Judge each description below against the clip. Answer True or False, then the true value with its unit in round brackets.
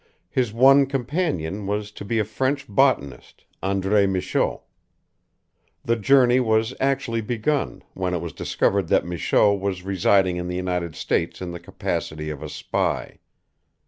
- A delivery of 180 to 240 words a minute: False (145 wpm)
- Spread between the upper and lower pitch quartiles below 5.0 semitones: False (5.5 semitones)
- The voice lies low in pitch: True (100 Hz)